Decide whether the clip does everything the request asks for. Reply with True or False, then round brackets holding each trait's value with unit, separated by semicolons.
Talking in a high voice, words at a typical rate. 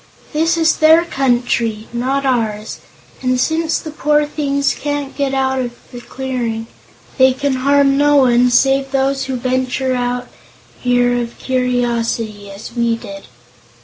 True (260 Hz; 145 wpm)